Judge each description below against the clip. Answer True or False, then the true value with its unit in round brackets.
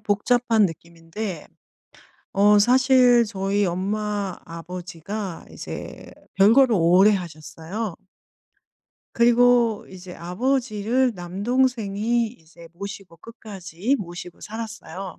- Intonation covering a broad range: False (4.5 semitones)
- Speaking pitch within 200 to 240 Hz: True (205 Hz)